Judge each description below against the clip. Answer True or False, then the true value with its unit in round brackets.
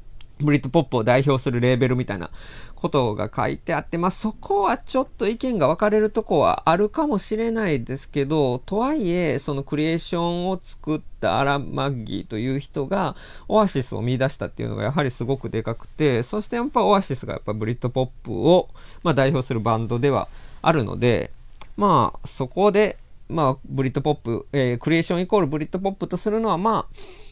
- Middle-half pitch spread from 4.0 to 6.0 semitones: False (6.8 semitones)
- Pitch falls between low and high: True (145 Hz)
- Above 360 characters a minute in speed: True (415 characters per minute)